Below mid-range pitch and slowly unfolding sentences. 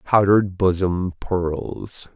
Yes: very low, 90 Hz; slow, 85 wpm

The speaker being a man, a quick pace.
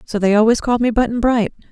No: female; fast, 245 wpm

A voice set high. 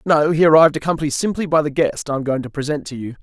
No: medium, 150 Hz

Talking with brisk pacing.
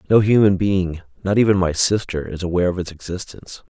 No: average, 190 wpm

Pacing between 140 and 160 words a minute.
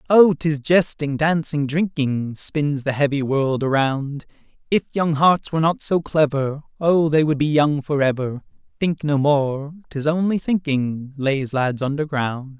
Yes: average, 155 wpm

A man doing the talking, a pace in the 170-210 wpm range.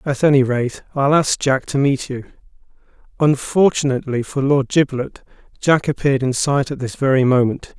No: male; average, 160 wpm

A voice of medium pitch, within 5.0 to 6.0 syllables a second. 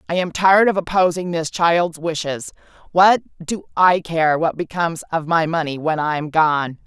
No: medium, 165 Hz; 4.8 syllables/s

